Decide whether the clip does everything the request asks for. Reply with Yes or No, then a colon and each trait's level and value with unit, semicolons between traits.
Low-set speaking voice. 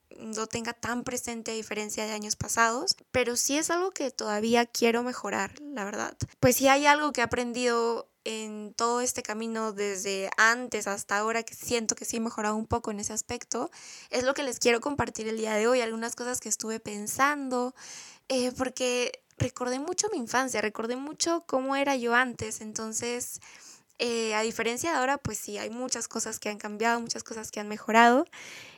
No: high, 235 Hz